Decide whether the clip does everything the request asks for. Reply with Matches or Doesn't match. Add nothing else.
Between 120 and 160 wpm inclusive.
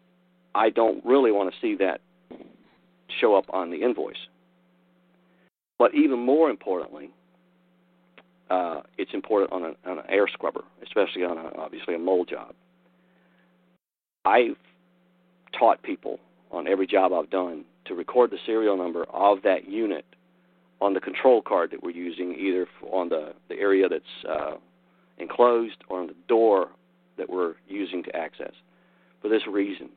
Matches